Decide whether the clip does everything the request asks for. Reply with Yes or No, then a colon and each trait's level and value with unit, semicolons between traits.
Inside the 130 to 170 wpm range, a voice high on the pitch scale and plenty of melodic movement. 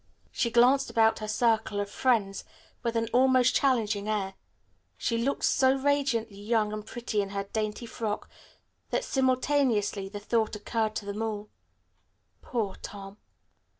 No: average, 145 wpm; high, 220 Hz; average, 3.1 semitones